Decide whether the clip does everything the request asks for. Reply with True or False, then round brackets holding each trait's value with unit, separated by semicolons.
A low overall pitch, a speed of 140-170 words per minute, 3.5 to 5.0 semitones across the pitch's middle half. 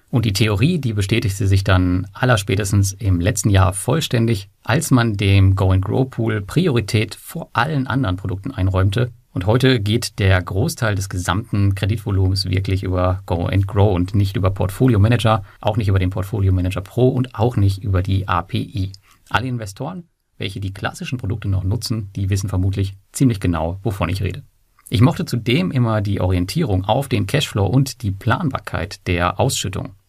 True (105 Hz; 160 wpm; 4.0 semitones)